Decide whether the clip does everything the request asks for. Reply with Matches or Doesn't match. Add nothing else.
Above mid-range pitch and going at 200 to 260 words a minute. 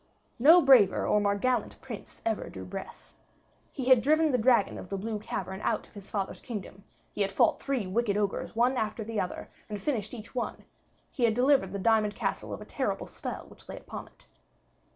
Matches